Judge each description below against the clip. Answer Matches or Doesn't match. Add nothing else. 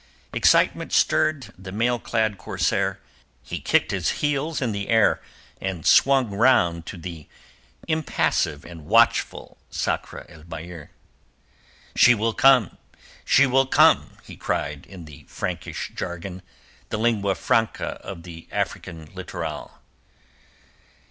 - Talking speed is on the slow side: Matches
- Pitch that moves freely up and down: Matches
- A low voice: Matches